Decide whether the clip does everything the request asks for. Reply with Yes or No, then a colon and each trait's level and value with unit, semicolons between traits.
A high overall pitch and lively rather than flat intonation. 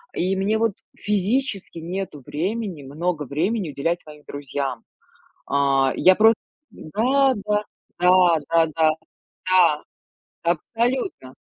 No: medium, 175 Hz; wide, 5.8 semitones